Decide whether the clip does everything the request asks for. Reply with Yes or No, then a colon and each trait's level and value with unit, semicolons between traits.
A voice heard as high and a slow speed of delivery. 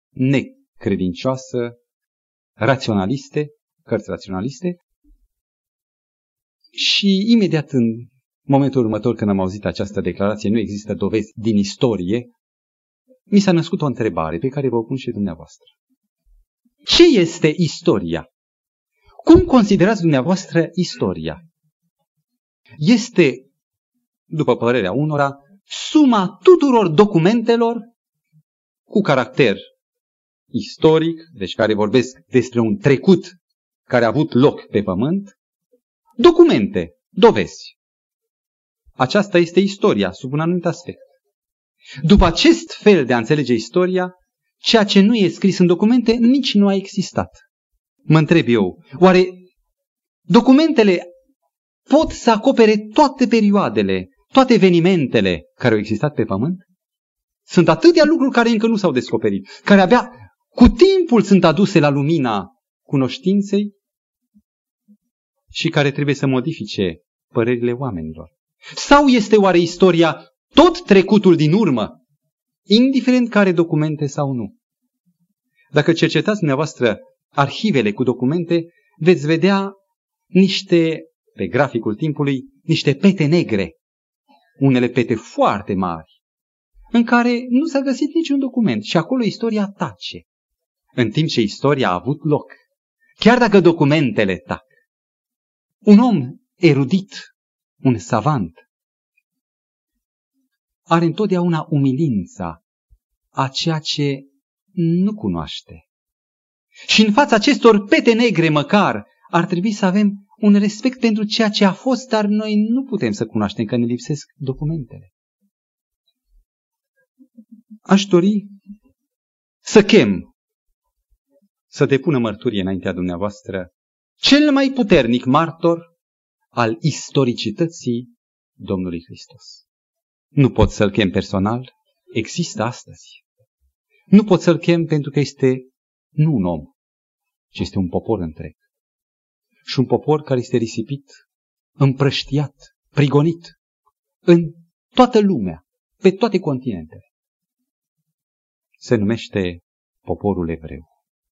No: medium, 170 Hz; slow, 110 wpm